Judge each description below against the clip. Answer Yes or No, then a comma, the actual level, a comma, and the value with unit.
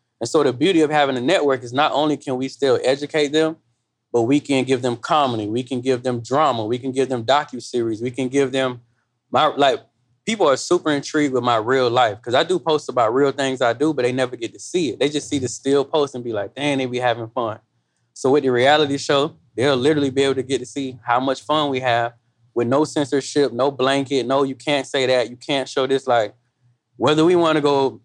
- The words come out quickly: Yes, fast, 245 wpm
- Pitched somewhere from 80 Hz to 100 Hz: No, low, 135 Hz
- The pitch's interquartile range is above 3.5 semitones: No, average, 2.9 semitones